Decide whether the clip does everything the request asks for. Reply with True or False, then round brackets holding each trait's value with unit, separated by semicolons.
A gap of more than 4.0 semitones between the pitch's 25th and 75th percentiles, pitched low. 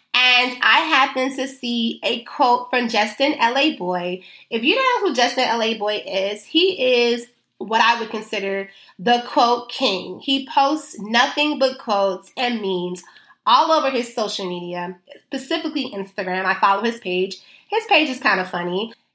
False (5.2 semitones; 235 Hz)